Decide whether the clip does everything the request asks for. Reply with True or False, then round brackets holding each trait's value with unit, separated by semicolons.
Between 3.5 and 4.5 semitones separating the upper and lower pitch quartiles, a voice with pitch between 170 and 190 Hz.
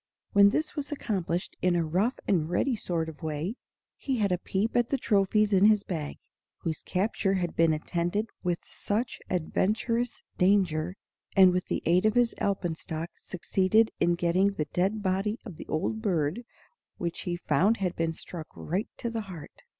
True (3.8 semitones; 185 Hz)